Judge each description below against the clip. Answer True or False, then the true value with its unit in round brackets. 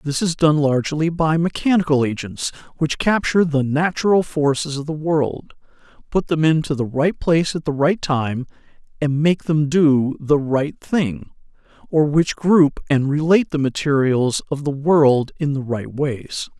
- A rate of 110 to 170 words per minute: True (165 wpm)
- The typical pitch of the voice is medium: True (150 Hz)